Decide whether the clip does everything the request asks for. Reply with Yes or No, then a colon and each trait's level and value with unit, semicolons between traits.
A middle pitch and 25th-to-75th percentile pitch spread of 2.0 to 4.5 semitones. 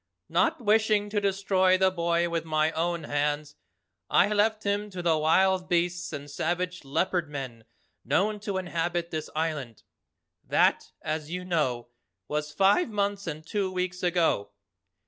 Yes: medium, 175 Hz; average, 3.7 semitones